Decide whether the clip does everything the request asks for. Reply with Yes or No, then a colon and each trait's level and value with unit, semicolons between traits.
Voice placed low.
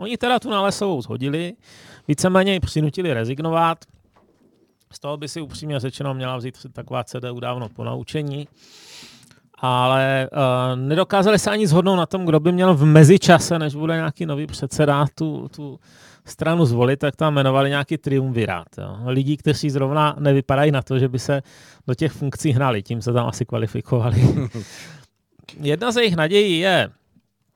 No: medium, 145 Hz